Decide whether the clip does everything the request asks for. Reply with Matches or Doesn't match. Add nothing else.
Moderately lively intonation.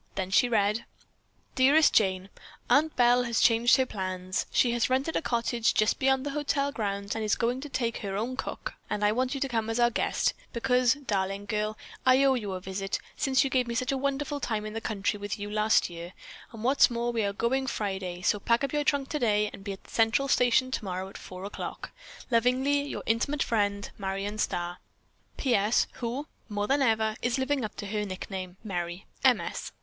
Matches